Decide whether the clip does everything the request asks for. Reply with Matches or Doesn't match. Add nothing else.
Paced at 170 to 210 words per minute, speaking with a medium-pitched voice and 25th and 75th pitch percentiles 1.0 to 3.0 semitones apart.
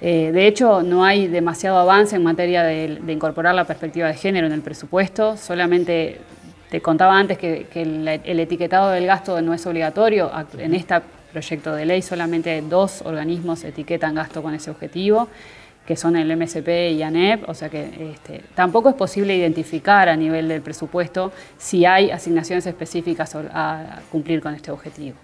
Matches